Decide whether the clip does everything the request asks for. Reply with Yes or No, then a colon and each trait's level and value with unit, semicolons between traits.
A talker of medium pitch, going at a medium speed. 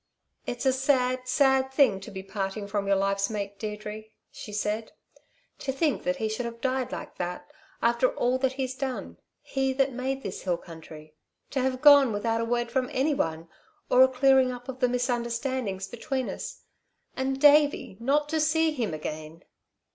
No: very high, 250 Hz; average, 180 wpm